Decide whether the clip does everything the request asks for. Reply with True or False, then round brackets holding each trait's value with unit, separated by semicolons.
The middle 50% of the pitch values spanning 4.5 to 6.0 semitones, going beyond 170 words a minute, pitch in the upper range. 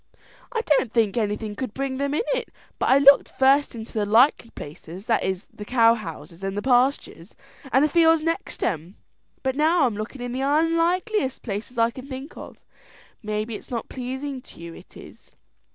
True (4.9 semitones; 190 wpm; 250 Hz)